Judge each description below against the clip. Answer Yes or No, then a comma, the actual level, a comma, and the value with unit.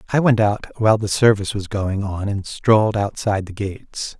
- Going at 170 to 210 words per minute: Yes, average, 200 wpm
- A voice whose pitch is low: Yes, low, 105 Hz